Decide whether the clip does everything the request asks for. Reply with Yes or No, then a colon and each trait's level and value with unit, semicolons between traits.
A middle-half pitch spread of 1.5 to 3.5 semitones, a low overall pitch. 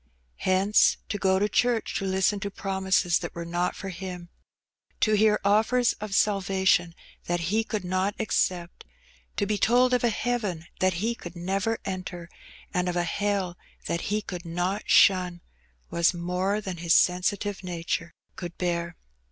No: average, 2.8 semitones; high, 190 Hz